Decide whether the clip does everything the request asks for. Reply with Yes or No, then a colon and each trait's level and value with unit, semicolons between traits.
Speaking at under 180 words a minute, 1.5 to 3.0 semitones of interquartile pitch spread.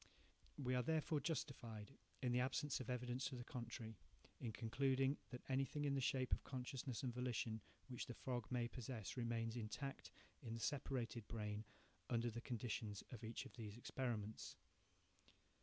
Yes: average, 160 wpm; narrow, 2.5 semitones